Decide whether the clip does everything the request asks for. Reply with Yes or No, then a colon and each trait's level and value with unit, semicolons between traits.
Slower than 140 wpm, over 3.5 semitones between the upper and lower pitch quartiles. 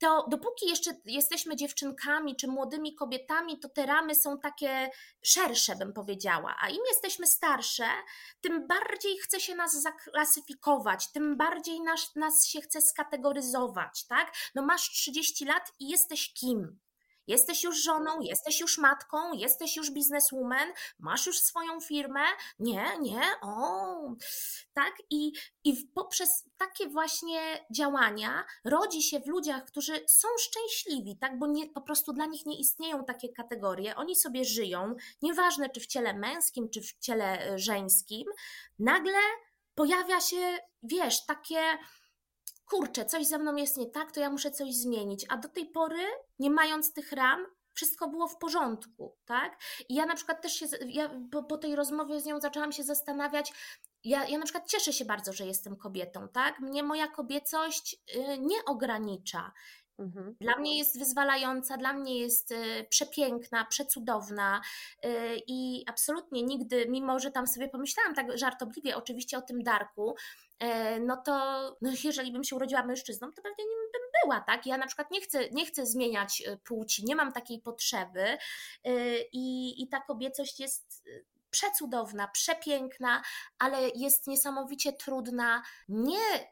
No: average, 150 wpm; average, 4.2 semitones